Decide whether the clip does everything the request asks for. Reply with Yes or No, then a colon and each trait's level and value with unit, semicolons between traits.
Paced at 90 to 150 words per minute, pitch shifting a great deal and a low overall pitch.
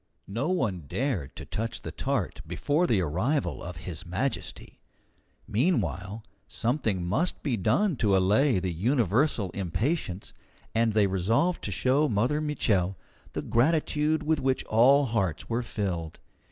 Yes: average, 140 wpm; wide, 7.2 semitones; low, 115 Hz